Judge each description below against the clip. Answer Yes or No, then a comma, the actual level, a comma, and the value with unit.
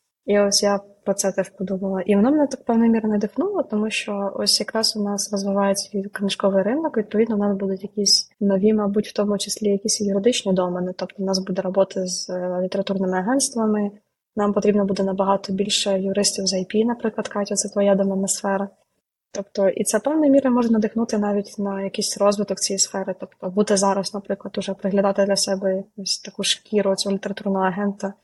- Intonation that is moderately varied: No, narrow, 1.4 semitones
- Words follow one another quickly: Yes, fast, 180 wpm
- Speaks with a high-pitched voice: Yes, high, 200 Hz